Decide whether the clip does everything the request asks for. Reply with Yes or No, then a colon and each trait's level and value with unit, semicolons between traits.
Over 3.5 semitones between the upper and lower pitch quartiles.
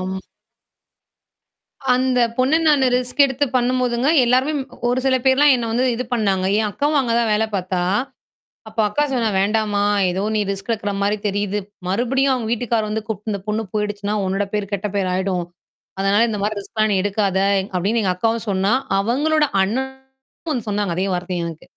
Yes: average, 4.1 semitones